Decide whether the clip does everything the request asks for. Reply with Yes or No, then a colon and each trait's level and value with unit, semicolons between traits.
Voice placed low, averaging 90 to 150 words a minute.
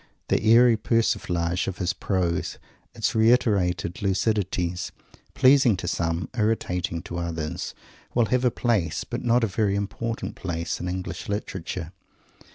Yes: very low, 95 Hz; slow, 135 wpm